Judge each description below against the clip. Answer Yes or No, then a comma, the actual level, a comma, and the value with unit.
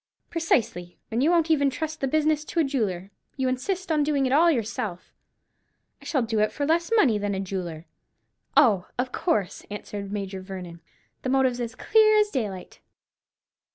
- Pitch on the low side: No, very high, 255 Hz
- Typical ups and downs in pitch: No, wide, 7.6 semitones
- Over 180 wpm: No, average, 175 wpm